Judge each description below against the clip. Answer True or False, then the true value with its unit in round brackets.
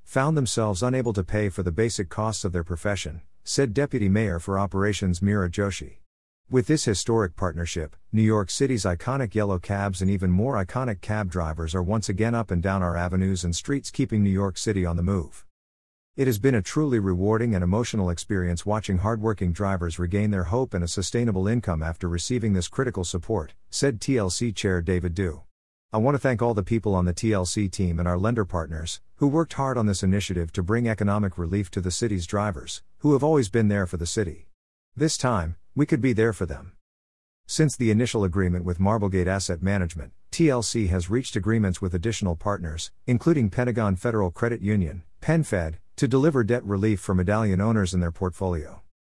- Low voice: True (100 Hz)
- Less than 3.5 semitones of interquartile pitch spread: False (4.2 semitones)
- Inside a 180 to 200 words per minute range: True (190 wpm)